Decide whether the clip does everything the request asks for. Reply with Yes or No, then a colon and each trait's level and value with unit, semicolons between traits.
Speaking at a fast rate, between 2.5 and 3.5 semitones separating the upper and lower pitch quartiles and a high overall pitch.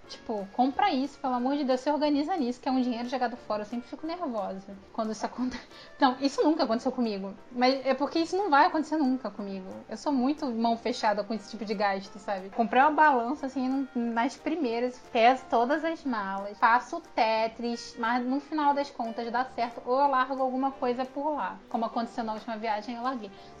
Yes: fast, 205 wpm; average, 3.1 semitones; high, 245 Hz